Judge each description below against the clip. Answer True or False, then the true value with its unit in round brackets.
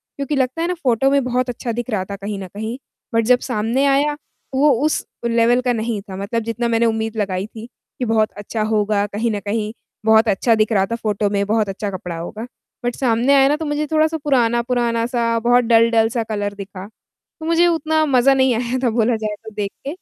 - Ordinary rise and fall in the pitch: True (3.0 semitones)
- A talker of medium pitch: False (230 Hz)